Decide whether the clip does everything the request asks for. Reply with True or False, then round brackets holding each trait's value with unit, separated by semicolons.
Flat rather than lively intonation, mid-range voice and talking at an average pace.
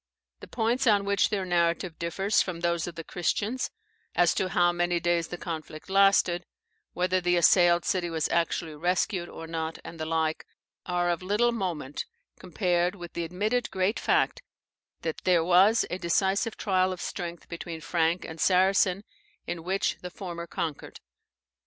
True (2.2 semitones; 175 Hz; 165 wpm)